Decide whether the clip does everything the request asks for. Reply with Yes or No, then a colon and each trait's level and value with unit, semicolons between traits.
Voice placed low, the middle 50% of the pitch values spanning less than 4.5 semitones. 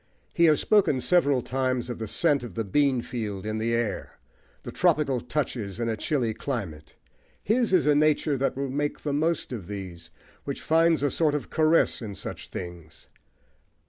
No: low, 130 Hz; wide, 5.4 semitones